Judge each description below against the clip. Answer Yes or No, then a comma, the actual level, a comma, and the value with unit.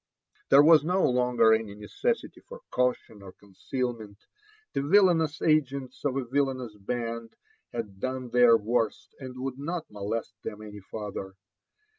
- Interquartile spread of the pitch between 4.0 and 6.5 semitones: Yes, average, 4.4 semitones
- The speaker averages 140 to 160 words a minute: Yes, average, 145 wpm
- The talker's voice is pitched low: Yes, low, 125 Hz